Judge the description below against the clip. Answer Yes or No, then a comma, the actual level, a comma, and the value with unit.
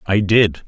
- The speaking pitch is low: Yes, low, 100 Hz